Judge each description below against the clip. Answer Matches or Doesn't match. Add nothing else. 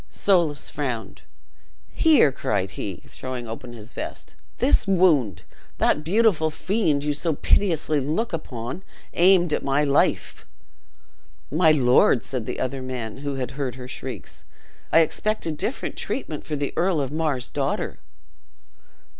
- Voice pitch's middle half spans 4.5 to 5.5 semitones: Matches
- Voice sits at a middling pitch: Matches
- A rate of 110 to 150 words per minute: Matches